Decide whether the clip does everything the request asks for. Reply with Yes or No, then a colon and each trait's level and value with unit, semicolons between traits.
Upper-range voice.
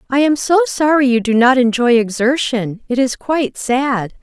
Yes: very high, 250 Hz